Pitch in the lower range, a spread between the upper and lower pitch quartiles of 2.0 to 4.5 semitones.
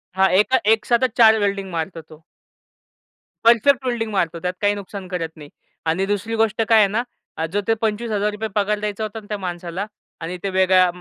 No: high, 205 Hz; average, 3.3 semitones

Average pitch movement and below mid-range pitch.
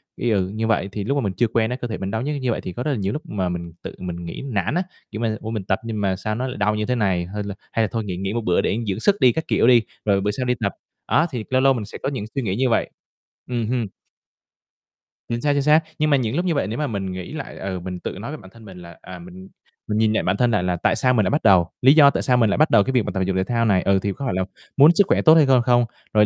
Yes: average, 4.8 semitones; low, 110 Hz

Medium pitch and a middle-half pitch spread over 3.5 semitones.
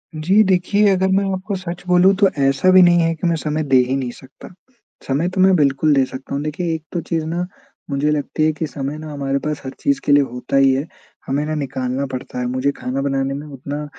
Yes: medium, 150 Hz; average, 4.2 semitones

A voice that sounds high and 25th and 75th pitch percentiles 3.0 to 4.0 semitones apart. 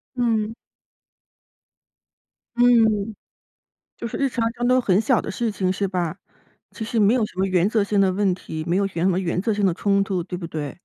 Yes: high, 200 Hz; average, 3.5 semitones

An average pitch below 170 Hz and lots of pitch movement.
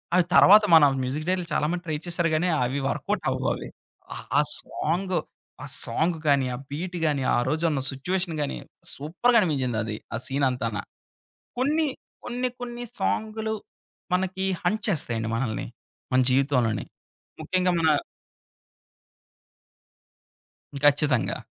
Yes: medium, 155 Hz; wide, 5.8 semitones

